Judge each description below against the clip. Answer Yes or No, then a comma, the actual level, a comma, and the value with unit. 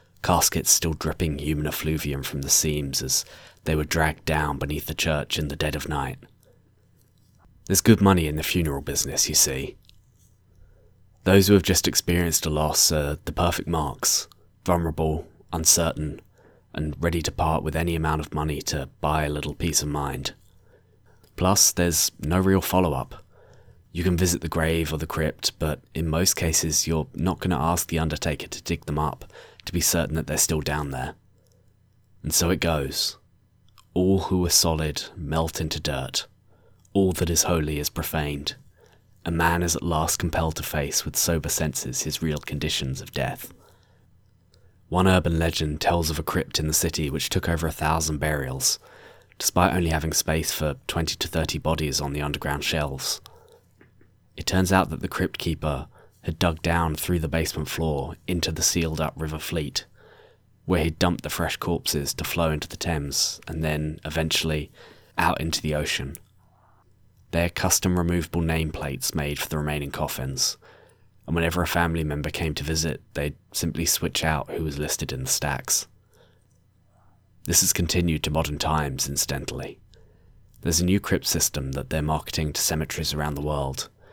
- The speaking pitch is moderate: No, very low, 80 Hz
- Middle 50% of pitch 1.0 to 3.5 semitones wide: Yes, average, 2.9 semitones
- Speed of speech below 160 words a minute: No, average, 175 wpm